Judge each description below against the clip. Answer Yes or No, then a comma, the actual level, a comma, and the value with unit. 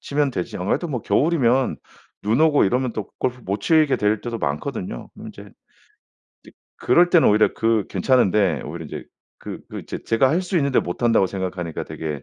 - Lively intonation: Yes, wide, 6.6 semitones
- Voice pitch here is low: Yes, low, 115 Hz